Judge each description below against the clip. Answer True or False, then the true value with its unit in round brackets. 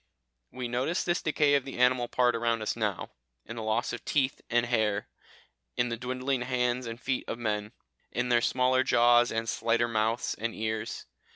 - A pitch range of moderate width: False (1.9 semitones)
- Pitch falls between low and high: False (120 Hz)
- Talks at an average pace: True (185 wpm)